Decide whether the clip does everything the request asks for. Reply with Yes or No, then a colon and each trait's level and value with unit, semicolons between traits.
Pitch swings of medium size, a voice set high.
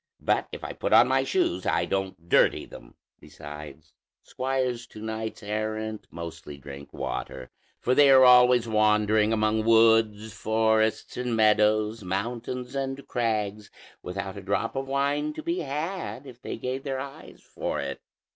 No: average, 3.6 semitones; low, 110 Hz